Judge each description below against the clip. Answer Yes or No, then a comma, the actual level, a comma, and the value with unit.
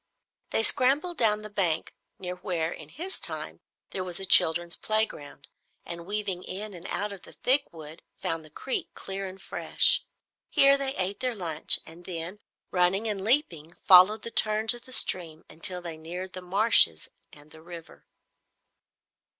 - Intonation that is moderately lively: Yes, average, 4.2 semitones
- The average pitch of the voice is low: No, medium, 185 Hz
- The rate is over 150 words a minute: Yes, average, 165 wpm